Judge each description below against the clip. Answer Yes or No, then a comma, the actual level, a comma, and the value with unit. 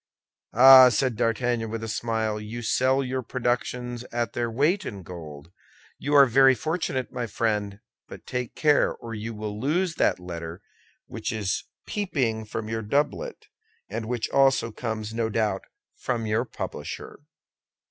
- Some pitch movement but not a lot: Yes, average, 3.2 semitones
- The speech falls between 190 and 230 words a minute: No, average, 150 wpm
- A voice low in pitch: Yes, low, 115 Hz